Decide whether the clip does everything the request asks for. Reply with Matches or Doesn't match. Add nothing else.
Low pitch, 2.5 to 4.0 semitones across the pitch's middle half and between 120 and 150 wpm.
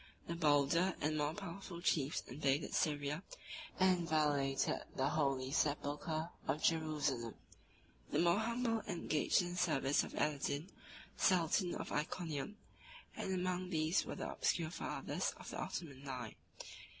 Doesn't match